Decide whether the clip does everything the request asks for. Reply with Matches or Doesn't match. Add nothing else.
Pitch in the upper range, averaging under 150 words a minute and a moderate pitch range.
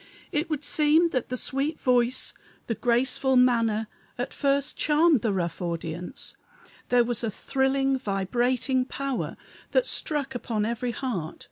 Matches